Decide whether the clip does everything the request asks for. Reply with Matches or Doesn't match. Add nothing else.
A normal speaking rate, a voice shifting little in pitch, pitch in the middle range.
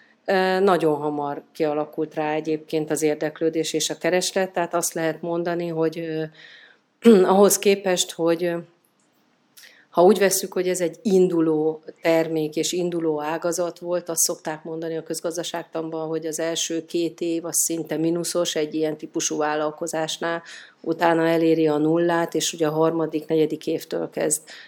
Matches